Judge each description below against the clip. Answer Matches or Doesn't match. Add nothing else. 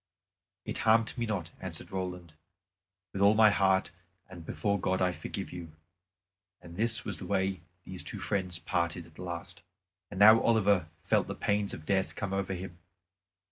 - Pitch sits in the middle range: Doesn't match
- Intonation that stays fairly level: Matches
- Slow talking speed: Doesn't match